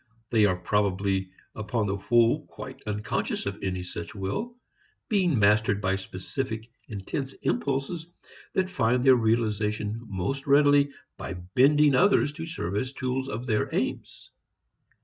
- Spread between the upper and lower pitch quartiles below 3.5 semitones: No, wide, 5.5 semitones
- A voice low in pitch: Yes, low, 115 Hz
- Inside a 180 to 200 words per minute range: No, slow, 135 wpm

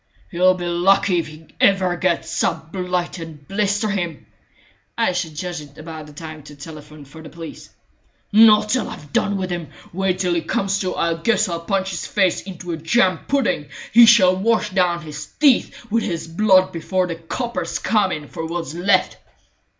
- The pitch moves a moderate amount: Yes, average, 3.2 semitones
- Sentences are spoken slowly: No, average, 185 wpm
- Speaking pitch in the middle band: Yes, medium, 180 Hz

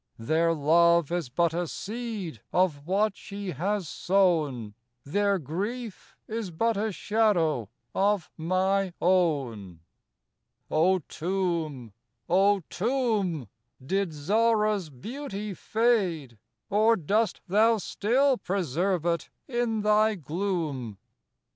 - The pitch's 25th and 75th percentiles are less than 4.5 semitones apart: No, average, 4.9 semitones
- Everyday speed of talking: No, slow, 105 wpm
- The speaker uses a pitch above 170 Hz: Yes, medium, 185 Hz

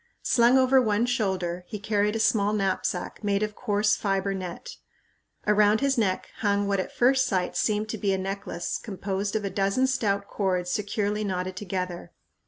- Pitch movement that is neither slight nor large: No, narrow, 2.1 semitones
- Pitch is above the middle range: Yes, high, 205 Hz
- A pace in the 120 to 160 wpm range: No, average, 175 wpm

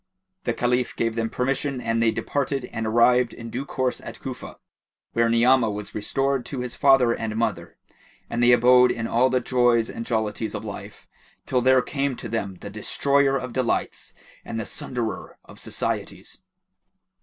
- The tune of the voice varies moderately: No, narrow, 2.2 semitones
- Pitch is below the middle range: Yes, low, 120 Hz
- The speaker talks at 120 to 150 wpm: No, average, 170 wpm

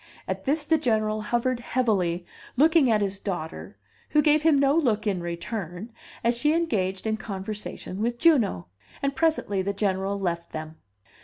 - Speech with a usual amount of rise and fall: No, wide, 6.3 semitones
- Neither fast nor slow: Yes, average, 160 wpm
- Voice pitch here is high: Yes, high, 215 Hz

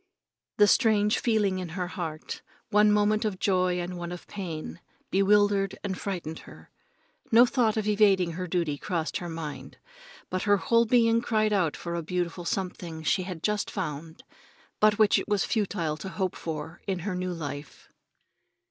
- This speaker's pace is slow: No, average, 170 wpm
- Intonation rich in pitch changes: No, average, 3.6 semitones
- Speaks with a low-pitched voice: No, medium, 185 Hz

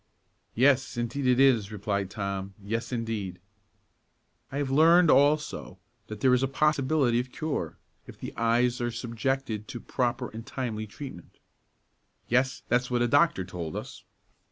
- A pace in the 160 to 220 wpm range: No, average, 150 wpm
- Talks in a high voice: No, low, 120 Hz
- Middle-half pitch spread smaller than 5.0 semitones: Yes, average, 3.8 semitones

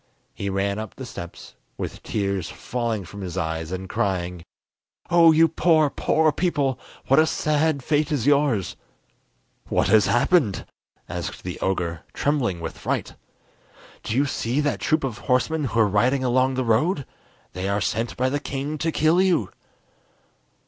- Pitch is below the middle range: Yes, low, 125 Hz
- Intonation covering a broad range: Yes, wide, 7.1 semitones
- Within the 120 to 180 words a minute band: Yes, average, 160 wpm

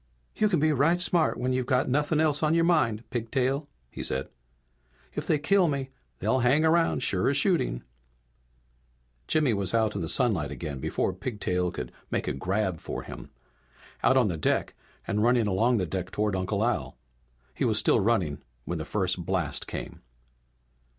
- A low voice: Yes, low, 115 Hz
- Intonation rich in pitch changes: Yes, wide, 7.6 semitones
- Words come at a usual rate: Yes, average, 175 wpm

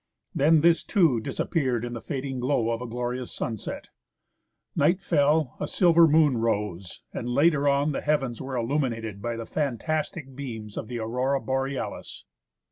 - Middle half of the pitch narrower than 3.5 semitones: No, average, 4.1 semitones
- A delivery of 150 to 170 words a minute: Yes, average, 160 wpm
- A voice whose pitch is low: Yes, low, 130 Hz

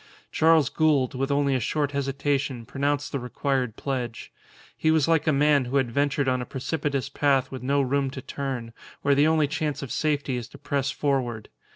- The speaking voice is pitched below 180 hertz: Yes, medium, 140 Hz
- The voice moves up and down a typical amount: No, narrow, 1.9 semitones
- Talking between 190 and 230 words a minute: Yes, average, 195 wpm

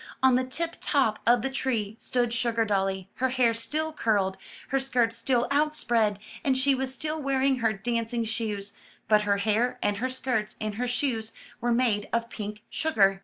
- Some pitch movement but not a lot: Yes, average, 3.5 semitones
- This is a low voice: No, high, 235 Hz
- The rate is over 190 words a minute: No, average, 175 wpm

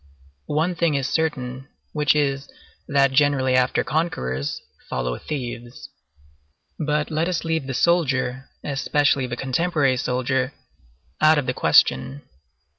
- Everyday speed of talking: No, slow, 120 wpm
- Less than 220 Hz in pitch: Yes, medium, 140 Hz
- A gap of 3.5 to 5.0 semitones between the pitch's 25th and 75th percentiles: No, average, 3.0 semitones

